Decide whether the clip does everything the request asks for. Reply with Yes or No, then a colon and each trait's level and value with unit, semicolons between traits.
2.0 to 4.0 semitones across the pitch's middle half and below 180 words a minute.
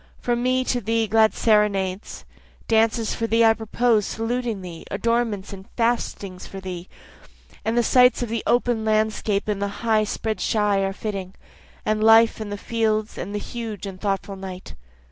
Yes: narrow, 2.5 semitones; average, 170 wpm